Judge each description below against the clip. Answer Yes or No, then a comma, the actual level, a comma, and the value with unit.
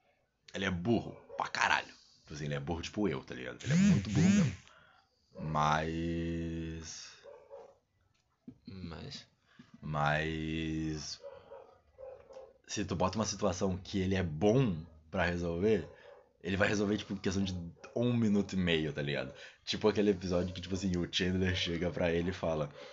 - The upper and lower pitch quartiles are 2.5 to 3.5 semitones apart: No, average, 4.3 semitones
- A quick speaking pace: No, average, 150 wpm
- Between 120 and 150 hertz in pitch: No, very low, 90 Hz